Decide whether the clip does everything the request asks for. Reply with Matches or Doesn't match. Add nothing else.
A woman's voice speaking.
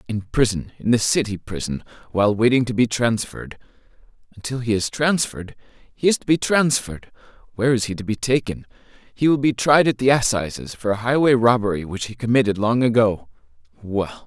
Doesn't match